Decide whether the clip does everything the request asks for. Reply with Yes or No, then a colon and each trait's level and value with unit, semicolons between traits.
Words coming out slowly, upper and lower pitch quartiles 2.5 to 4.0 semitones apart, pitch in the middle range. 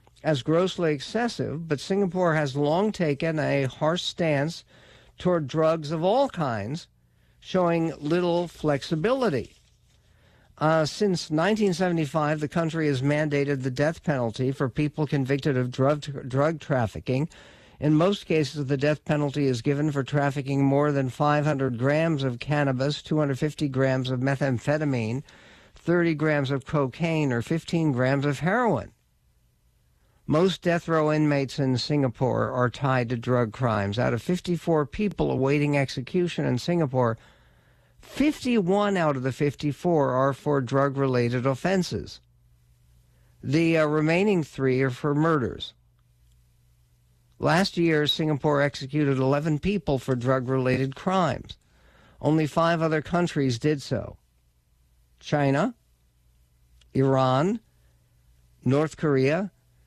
Yes: slow, 120 wpm; average, 3.7 semitones; medium, 145 Hz